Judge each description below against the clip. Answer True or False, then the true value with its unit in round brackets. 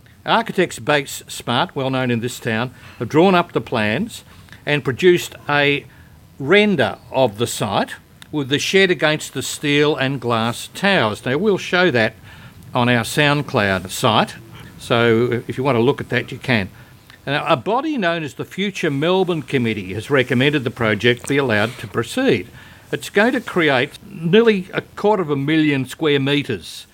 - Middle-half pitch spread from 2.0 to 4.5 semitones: False (5.3 semitones)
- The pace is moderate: True (170 wpm)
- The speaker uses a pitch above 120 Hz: True (135 Hz)